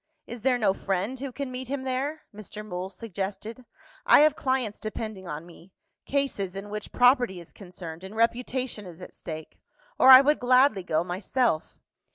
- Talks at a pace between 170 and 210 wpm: Yes, average, 175 wpm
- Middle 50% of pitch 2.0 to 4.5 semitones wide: No, average, 5.3 semitones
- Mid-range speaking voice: No, high, 215 Hz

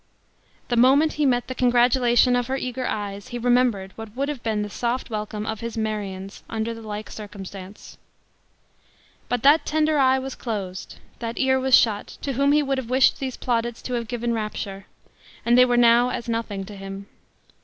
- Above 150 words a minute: Yes, average, 190 wpm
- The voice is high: Yes, high, 235 Hz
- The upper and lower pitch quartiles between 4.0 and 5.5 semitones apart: No, average, 3.4 semitones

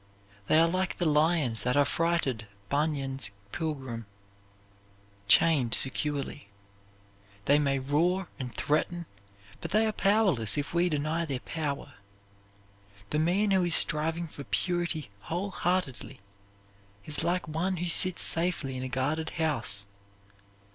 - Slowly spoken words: Yes, slow, 125 wpm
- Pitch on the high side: No, medium, 155 Hz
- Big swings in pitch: No, average, 4.0 semitones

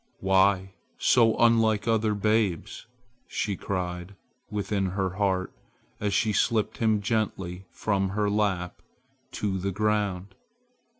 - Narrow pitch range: Yes, narrow, 2.1 semitones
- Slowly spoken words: Yes, slow, 115 wpm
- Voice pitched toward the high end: No, low, 100 Hz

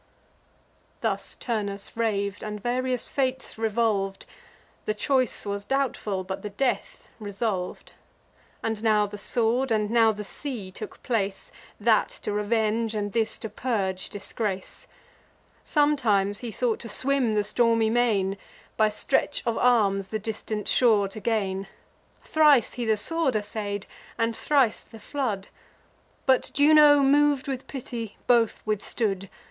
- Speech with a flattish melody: No, average, 3.4 semitones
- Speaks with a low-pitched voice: No, high, 220 Hz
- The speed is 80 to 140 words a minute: Yes, slow, 135 wpm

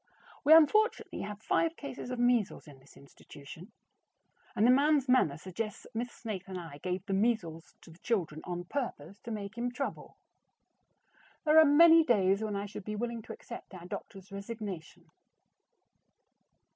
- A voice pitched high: Yes, high, 210 Hz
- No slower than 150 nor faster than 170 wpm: Yes, average, 165 wpm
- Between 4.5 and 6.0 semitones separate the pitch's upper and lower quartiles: Yes, average, 5.2 semitones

